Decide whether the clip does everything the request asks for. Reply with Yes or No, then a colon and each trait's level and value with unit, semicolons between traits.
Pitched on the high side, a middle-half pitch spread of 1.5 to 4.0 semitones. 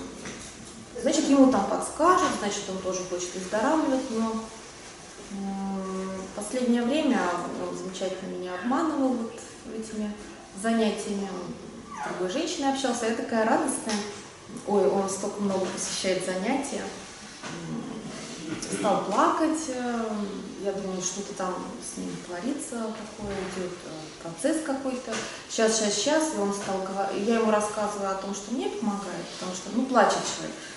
No: high, 210 Hz; average, 4.5 semitones